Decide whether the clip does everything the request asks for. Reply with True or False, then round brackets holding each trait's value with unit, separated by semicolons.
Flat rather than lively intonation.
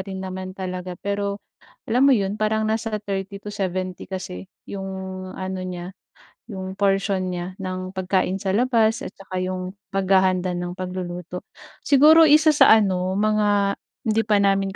True (2.0 semitones)